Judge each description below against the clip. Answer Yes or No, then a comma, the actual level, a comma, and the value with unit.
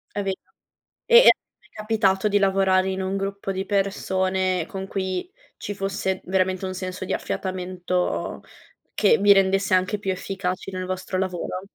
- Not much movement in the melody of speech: Yes, narrow, 0.9 semitones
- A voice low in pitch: No, high, 190 Hz